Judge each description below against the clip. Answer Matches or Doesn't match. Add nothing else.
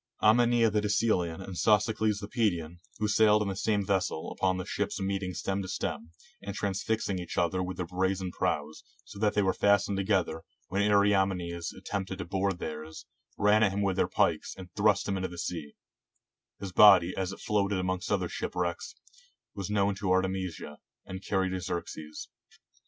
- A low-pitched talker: Matches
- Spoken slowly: Doesn't match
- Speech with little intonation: Matches